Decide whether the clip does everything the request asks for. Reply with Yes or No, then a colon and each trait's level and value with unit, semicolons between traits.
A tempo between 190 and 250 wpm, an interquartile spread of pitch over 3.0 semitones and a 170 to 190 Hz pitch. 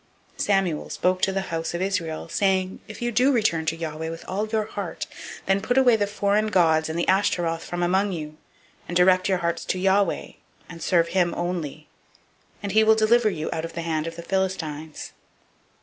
Yes: fast, 205 wpm; average, 3.4 semitones; medium, 185 Hz